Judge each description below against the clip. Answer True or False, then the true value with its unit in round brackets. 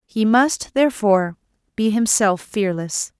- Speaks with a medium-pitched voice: False (215 Hz)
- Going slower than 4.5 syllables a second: True (4.2 syllables/s)